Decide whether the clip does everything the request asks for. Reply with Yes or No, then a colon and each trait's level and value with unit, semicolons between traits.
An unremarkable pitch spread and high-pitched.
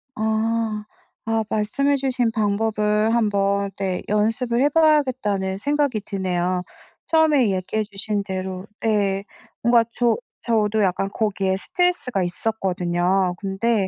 Yes: average, 3.2 semitones; high, 210 Hz